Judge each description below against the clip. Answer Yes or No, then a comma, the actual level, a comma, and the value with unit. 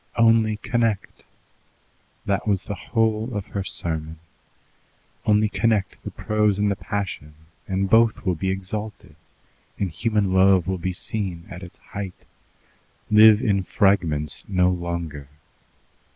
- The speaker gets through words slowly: Yes, slow, 130 wpm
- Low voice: Yes, low, 100 Hz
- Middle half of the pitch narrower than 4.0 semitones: Yes, average, 2.8 semitones